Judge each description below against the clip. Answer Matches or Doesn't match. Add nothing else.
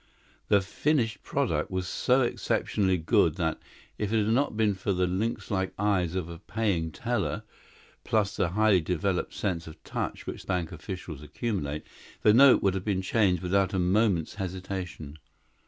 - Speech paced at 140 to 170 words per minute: Matches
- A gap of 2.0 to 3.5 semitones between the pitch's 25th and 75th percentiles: Matches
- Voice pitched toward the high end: Doesn't match